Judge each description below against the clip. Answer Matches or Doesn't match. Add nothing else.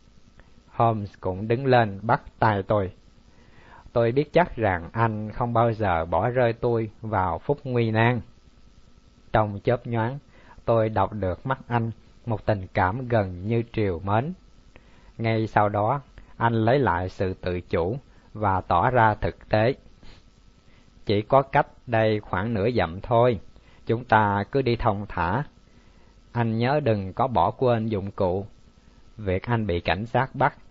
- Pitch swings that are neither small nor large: Matches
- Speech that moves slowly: Matches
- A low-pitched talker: Matches